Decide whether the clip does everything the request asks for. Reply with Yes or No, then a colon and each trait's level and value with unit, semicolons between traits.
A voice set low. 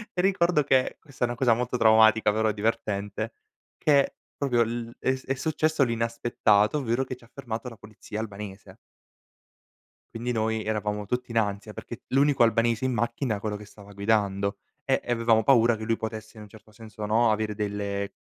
Yes: low, 115 Hz